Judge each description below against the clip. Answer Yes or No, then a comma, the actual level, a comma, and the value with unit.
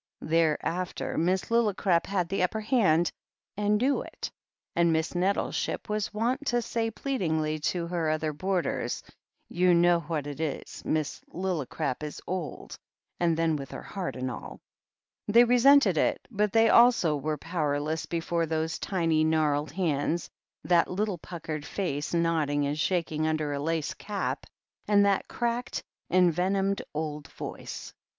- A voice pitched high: No, medium, 170 Hz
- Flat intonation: No, average, 4.2 semitones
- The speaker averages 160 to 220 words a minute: No, average, 150 wpm